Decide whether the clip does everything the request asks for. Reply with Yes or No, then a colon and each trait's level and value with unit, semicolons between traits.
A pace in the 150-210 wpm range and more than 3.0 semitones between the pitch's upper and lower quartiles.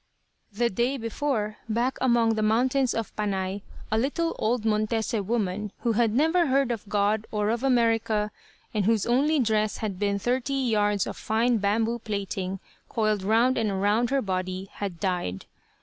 No: average, 165 wpm; average, 2.7 semitones